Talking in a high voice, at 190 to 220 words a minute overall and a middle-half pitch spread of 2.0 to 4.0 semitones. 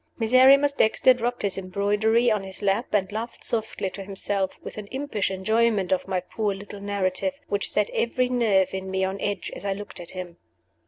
Yes: high, 205 Hz; average, 195 wpm; average, 3.2 semitones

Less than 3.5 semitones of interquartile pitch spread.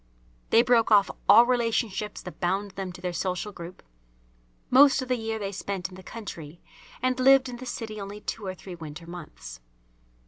No: average, 4.5 semitones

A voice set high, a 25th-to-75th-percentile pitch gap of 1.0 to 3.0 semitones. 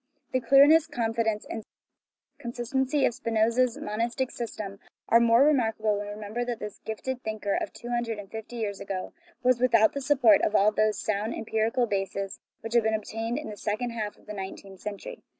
Yes: high, 225 Hz; narrow, 2.4 semitones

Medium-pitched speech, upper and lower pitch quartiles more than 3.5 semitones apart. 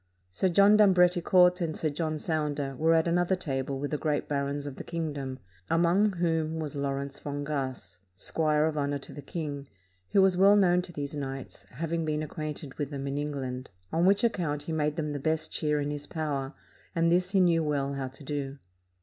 No: medium, 150 Hz; average, 3.1 semitones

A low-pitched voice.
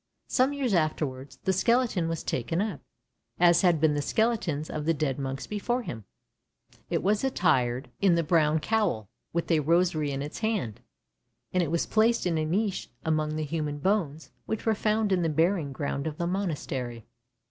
No: medium, 165 Hz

